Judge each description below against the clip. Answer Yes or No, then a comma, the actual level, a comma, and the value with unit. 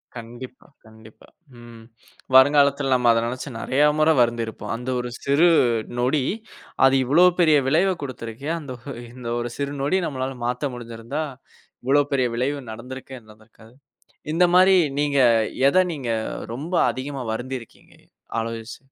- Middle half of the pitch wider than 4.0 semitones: No, average, 3.4 semitones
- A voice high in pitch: No, low, 130 Hz